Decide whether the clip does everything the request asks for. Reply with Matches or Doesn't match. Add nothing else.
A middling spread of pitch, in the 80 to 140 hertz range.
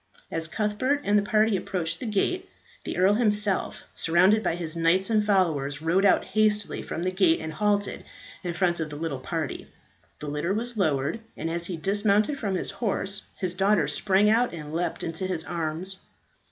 Doesn't match